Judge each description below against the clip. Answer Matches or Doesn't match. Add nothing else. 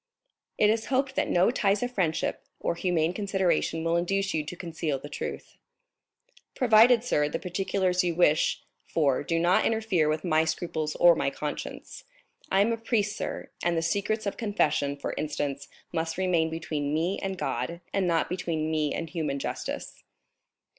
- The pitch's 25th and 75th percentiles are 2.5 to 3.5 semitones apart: Doesn't match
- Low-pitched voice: Doesn't match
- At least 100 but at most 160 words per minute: Doesn't match